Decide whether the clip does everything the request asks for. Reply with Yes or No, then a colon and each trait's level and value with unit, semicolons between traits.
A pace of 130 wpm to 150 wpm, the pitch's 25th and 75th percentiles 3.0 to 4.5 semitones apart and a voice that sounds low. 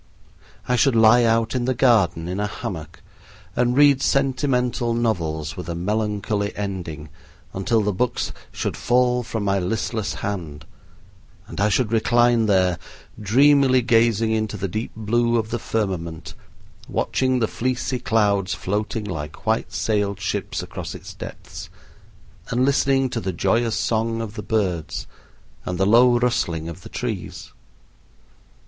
Yes: average, 145 wpm; average, 4.0 semitones; low, 110 Hz